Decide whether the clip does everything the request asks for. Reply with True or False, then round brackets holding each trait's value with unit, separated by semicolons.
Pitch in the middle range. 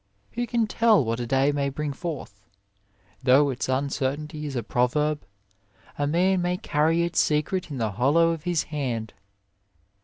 True (145 Hz)